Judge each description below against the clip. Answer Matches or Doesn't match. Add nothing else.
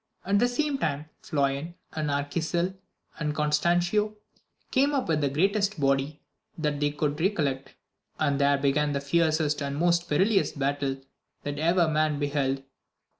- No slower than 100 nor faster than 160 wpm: Matches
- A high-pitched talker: Doesn't match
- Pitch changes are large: Doesn't match